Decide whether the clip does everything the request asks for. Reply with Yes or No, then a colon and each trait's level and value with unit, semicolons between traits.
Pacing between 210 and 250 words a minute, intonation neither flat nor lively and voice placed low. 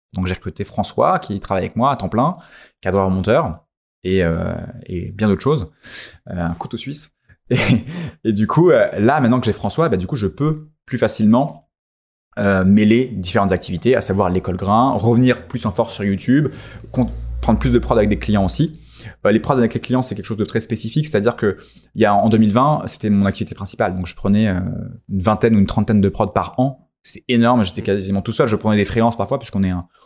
Yes: fast, 220 wpm; average, 3.8 semitones; low, 110 Hz